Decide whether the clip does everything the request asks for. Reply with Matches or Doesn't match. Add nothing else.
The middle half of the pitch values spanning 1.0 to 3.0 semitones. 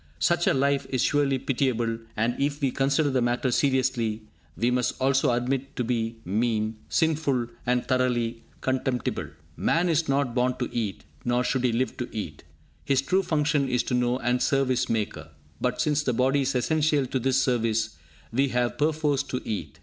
Matches